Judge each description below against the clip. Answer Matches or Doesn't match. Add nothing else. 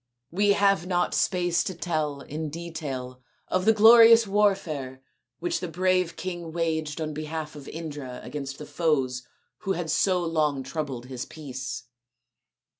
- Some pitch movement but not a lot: Matches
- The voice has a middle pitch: Matches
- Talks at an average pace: Matches